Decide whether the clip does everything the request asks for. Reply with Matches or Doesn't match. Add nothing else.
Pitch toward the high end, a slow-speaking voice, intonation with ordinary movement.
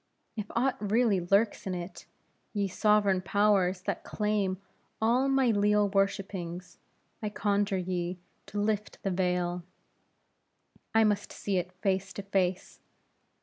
Doesn't match